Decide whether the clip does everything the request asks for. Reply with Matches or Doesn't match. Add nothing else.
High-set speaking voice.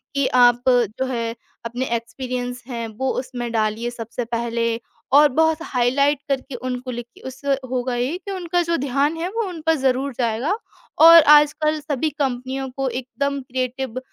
Matches